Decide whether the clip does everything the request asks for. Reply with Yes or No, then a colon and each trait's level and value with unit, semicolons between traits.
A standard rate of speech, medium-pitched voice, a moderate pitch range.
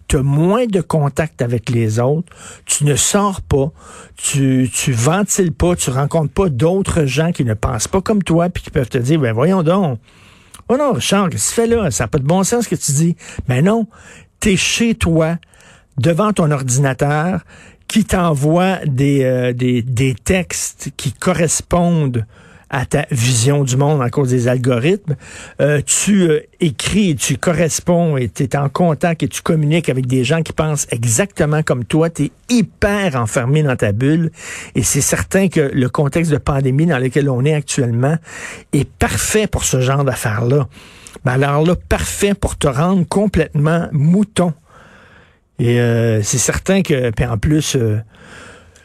Yes: average, 180 wpm; medium, 150 Hz; average, 5.0 semitones